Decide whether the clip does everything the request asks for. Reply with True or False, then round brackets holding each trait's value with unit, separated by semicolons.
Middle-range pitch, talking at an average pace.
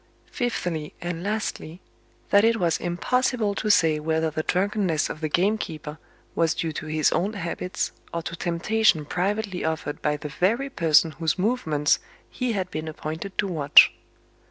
True (170 Hz; 155 wpm)